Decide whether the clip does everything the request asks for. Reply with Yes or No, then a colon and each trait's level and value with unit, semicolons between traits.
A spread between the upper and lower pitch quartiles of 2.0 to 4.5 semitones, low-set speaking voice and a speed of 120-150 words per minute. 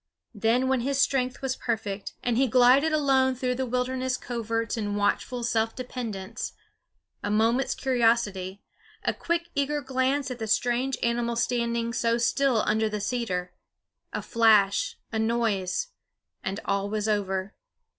No: average, 3.2 semitones; high, 235 Hz; average, 145 wpm